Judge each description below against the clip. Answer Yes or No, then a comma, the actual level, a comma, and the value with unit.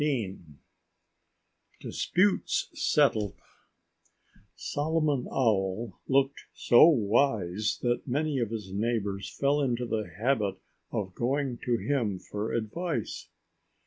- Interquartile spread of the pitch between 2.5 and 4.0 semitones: No, average, 5.0 semitones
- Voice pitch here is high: No, low, 120 Hz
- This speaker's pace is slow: Yes, slow, 100 wpm